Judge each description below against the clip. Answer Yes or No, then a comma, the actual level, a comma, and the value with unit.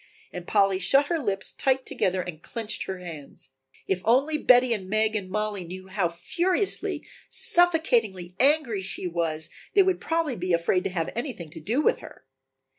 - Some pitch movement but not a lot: No, wide, 6.9 semitones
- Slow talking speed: No, average, 175 wpm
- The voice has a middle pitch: No, high, 205 Hz